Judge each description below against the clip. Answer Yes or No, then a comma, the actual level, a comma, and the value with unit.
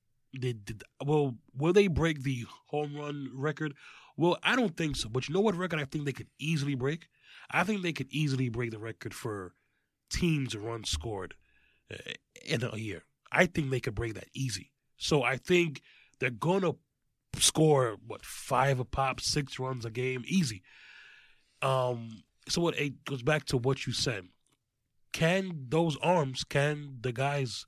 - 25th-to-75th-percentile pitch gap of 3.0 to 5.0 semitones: Yes, average, 4.0 semitones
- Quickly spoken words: No, average, 170 wpm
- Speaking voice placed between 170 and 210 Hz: No, low, 135 Hz